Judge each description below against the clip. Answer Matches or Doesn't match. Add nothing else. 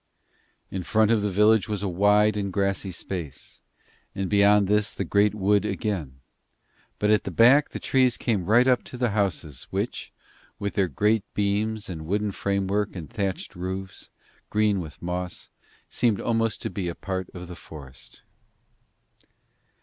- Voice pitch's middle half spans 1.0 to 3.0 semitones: Matches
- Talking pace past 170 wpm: Doesn't match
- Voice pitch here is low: Matches